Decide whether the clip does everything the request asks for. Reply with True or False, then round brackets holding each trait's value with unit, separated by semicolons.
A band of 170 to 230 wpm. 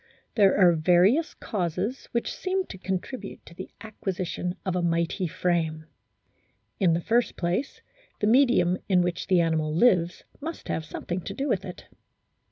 False (160 wpm)